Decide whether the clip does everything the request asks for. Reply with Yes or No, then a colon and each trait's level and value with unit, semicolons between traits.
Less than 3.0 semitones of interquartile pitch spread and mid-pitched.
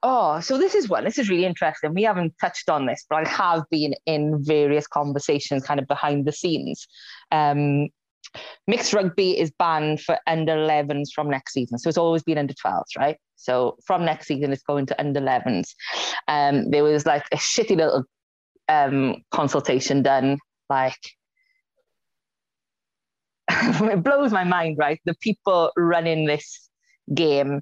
No: average, 3.6 semitones; medium, 155 Hz